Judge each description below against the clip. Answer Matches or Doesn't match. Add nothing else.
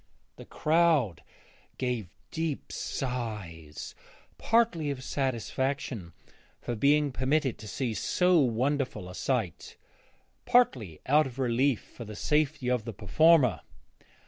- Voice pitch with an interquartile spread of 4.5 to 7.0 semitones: Matches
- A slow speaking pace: Matches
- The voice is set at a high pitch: Doesn't match